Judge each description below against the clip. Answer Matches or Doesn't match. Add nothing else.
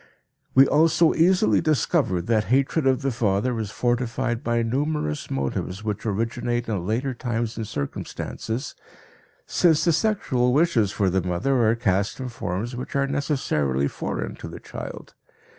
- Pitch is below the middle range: Matches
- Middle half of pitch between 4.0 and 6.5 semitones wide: Matches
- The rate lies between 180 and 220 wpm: Doesn't match